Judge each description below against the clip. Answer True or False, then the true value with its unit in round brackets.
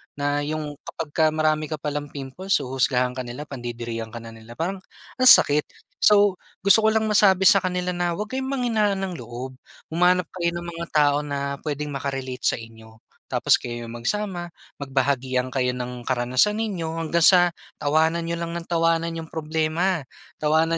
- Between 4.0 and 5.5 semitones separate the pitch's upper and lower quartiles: True (5.2 semitones)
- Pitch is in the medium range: True (155 Hz)